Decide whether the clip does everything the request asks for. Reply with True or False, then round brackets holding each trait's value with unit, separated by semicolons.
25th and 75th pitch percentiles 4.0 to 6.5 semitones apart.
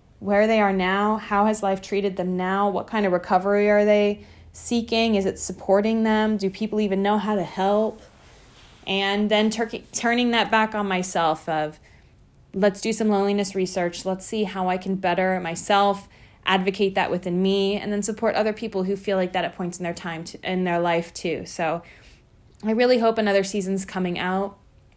False (2.4 semitones)